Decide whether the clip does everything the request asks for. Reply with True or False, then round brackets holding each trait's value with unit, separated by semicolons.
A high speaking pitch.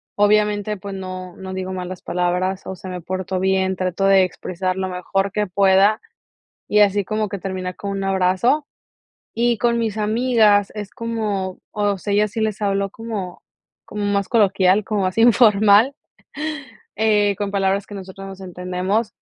True (195 Hz)